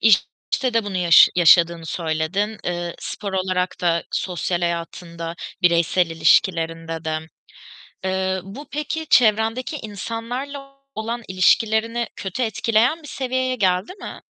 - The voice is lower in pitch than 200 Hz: Yes, high, 190 Hz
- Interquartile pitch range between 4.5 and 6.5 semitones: Yes, average, 5.1 semitones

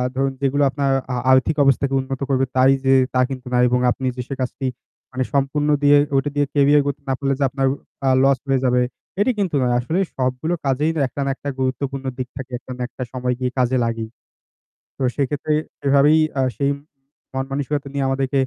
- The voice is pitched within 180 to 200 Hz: No, low, 135 Hz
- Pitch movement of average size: No, narrow, 1.6 semitones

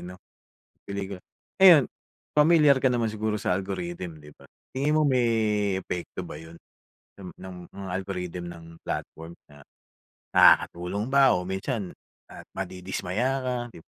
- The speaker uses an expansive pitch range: Yes, wide, 5.9 semitones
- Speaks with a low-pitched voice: Yes, low, 100 Hz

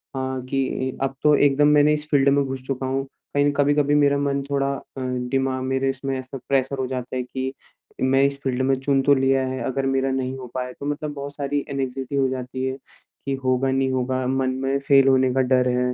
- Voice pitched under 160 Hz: Yes, low, 135 Hz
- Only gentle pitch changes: Yes, narrow, 1.1 semitones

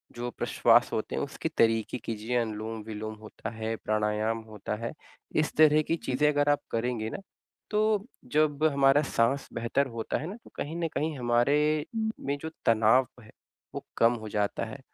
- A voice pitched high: No, low, 120 Hz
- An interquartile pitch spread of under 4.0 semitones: No, average, 4.6 semitones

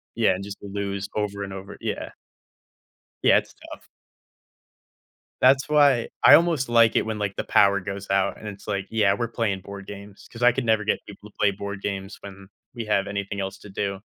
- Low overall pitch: Yes, low, 100 Hz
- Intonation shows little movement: Yes, narrow, 2.0 semitones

